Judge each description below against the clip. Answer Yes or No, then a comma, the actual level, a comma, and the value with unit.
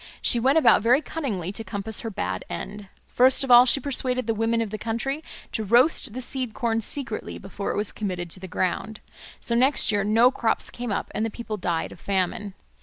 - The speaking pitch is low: No, high, 225 Hz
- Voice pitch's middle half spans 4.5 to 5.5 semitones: No, average, 3.7 semitones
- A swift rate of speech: Yes, fast, 215 wpm